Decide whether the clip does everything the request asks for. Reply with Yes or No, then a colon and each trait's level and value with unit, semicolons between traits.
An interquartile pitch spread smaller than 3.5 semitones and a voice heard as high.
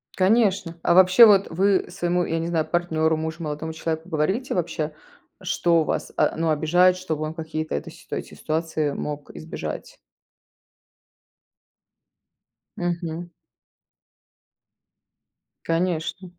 No: narrow, 2.4 semitones; medium, 165 Hz